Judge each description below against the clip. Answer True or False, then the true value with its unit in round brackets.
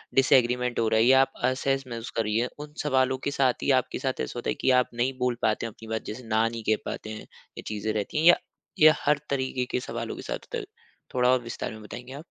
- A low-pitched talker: True (125 Hz)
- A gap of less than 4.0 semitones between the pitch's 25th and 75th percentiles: True (2.8 semitones)